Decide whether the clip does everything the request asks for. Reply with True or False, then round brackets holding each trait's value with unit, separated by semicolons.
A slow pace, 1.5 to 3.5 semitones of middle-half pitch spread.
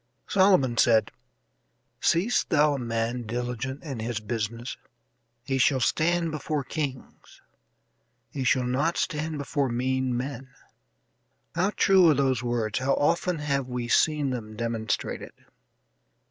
False (125 wpm; 3.9 semitones)